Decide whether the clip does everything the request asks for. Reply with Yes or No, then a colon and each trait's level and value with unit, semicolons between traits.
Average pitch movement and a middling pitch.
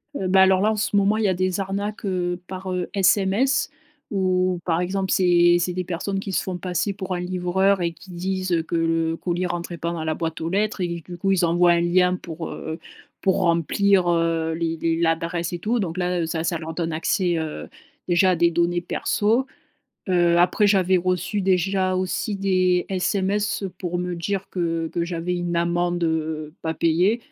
No: narrow, 2.0 semitones; medium, 180 Hz